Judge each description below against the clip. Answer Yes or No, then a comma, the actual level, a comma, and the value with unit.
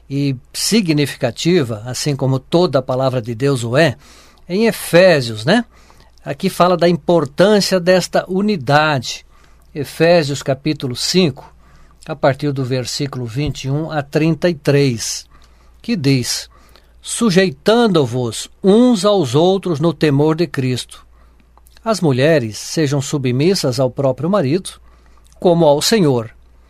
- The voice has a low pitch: No, medium, 145 Hz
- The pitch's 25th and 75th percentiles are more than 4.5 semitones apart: Yes, wide, 5.4 semitones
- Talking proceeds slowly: Yes, slow, 115 wpm